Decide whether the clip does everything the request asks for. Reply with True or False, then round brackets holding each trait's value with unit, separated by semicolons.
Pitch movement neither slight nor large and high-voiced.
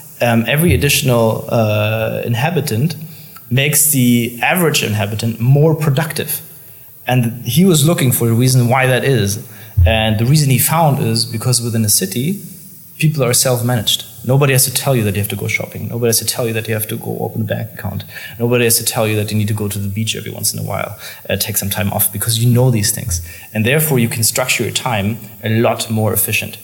False (3.5 semitones; 120 Hz)